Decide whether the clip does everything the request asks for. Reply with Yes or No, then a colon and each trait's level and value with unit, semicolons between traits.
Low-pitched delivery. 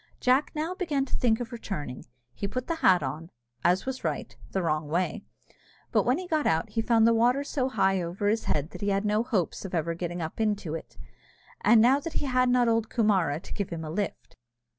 No: high, 210 Hz